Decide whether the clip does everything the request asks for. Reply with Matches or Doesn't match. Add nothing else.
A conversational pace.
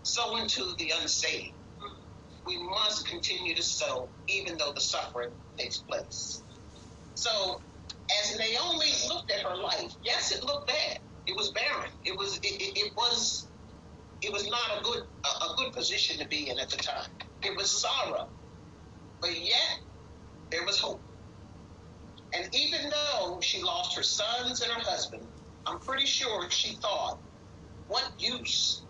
Matches